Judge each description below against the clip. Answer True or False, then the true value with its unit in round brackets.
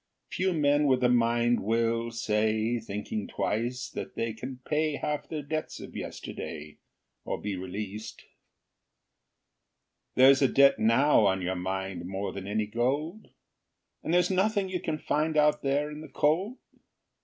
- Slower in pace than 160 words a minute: True (150 wpm)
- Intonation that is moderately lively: False (6.0 semitones)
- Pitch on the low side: True (120 Hz)